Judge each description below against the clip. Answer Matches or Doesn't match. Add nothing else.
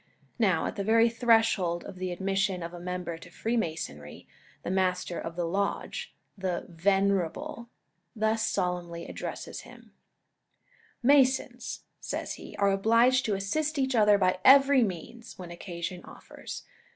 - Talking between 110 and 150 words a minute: Matches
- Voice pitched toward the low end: Doesn't match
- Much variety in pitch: Doesn't match